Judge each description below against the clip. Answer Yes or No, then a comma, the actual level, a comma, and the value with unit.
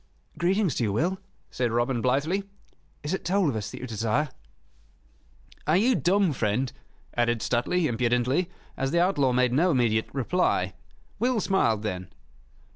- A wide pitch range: Yes, wide, 7.3 semitones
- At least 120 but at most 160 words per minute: Yes, average, 150 wpm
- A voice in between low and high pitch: No, low, 130 Hz